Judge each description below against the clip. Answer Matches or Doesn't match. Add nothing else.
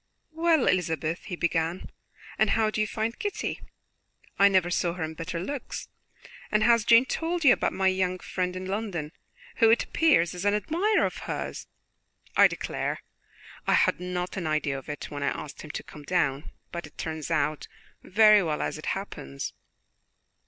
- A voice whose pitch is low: Doesn't match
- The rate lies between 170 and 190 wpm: Matches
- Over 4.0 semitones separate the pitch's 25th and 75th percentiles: Matches